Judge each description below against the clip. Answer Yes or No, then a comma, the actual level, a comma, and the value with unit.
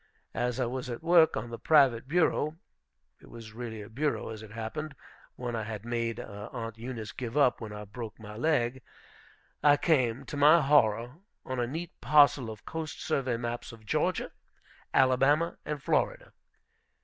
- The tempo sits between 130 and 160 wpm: No, average, 170 wpm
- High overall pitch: No, low, 125 Hz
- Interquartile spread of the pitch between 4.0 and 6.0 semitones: Yes, average, 4.4 semitones